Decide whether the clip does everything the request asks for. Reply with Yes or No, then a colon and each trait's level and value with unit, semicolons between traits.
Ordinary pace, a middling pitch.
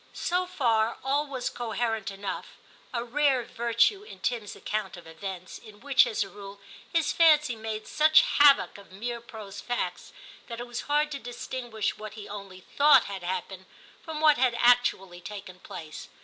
No: average, 170 wpm; high, 235 Hz